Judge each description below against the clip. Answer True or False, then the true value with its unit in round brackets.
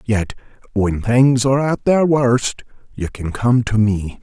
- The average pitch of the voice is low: True (120 Hz)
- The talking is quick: False (170 wpm)